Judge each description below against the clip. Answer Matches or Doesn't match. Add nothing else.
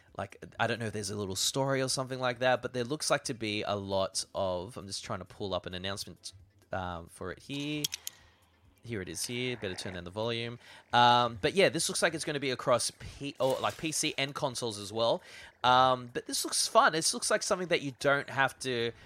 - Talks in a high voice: Doesn't match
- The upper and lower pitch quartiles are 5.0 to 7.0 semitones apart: Matches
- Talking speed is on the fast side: Matches